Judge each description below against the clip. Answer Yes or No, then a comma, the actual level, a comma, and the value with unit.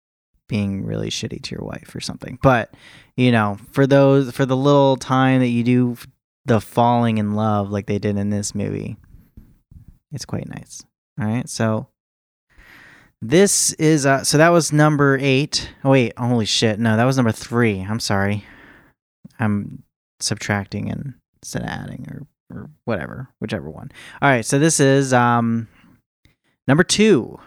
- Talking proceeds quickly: No, average, 160 wpm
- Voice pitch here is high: No, low, 120 Hz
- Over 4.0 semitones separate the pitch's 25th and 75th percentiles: Yes, average, 4.6 semitones